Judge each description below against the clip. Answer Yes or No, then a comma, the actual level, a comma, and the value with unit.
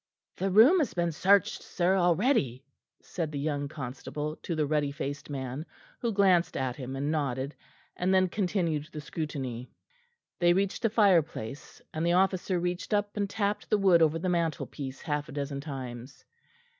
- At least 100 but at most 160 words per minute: No, average, 170 wpm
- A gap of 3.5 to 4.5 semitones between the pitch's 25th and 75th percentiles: No, average, 5.0 semitones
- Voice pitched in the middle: Yes, medium, 160 Hz